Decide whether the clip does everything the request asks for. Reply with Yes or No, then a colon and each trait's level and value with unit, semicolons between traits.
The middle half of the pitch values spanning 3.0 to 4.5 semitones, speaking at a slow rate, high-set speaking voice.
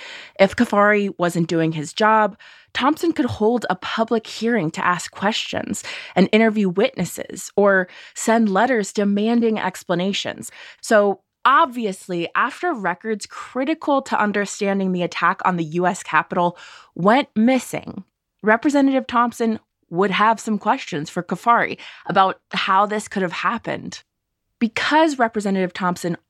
Yes: average, 4.1 semitones; slow, 125 wpm; high, 210 Hz